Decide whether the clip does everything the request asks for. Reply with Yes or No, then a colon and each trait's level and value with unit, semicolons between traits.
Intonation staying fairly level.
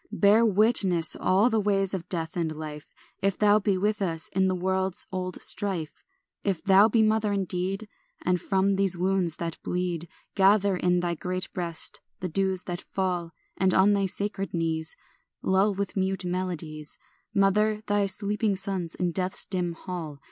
Yes: narrow, 2.2 semitones